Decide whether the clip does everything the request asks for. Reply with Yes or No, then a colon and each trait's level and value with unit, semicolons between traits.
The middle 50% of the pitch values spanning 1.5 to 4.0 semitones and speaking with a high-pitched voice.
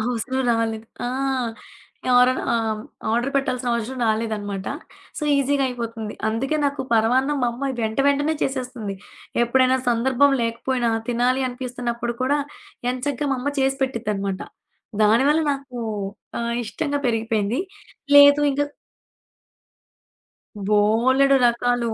Yes: average, 2.8 semitones; high, 245 Hz